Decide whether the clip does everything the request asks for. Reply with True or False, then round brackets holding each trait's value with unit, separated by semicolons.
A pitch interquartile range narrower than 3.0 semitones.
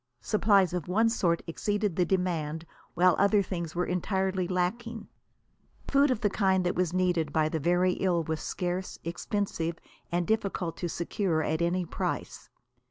True (2.6 semitones)